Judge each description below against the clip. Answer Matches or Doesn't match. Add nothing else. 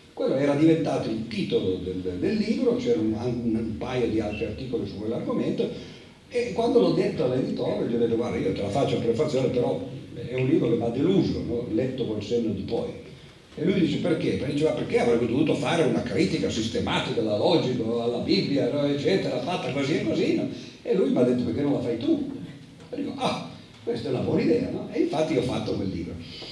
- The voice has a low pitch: Matches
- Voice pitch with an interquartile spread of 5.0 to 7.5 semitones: Matches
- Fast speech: Matches